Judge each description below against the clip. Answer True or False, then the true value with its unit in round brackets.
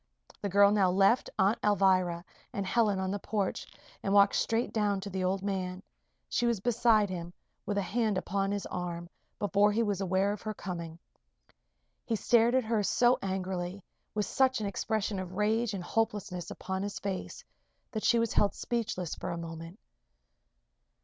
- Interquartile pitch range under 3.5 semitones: True (2.6 semitones)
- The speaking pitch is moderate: False (200 Hz)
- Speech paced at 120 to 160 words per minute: False (175 wpm)